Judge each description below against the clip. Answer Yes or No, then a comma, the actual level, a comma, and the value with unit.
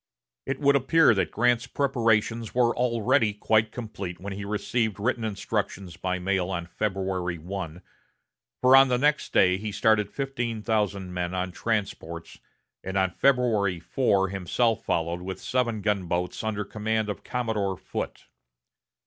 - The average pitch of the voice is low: Yes, low, 105 Hz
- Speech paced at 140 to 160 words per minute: Yes, average, 145 wpm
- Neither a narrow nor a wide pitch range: Yes, average, 4.0 semitones